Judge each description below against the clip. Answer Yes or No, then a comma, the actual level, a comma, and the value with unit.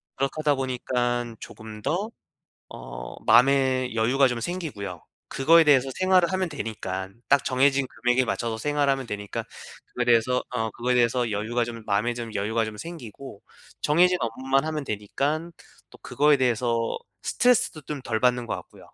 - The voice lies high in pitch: No, low, 125 Hz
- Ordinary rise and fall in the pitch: Yes, average, 3.8 semitones